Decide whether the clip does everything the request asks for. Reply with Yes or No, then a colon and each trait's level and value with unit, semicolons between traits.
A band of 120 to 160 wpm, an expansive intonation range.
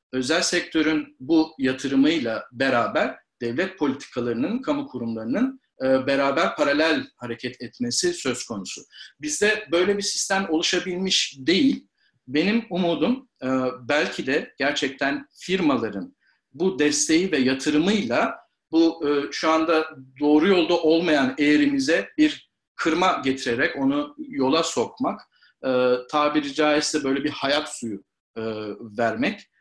No: average, 105 wpm; wide, 7.2 semitones